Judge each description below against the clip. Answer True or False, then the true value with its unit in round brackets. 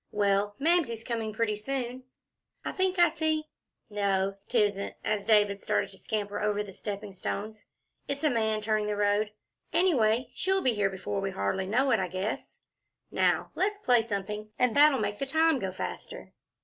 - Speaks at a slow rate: False (175 wpm)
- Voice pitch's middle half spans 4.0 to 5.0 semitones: True (4.3 semitones)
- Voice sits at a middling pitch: False (215 Hz)